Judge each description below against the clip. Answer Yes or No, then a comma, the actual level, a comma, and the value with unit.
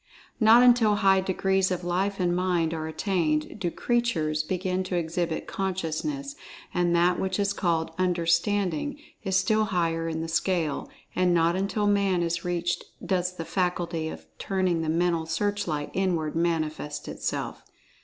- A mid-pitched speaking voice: Yes, medium, 180 Hz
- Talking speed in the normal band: Yes, average, 155 wpm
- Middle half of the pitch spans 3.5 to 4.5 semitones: No, average, 2.7 semitones